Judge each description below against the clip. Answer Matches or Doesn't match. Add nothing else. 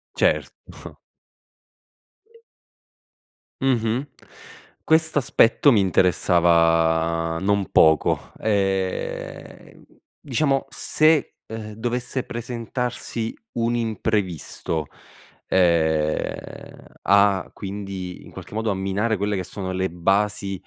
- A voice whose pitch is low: Matches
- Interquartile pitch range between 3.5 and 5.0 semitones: Matches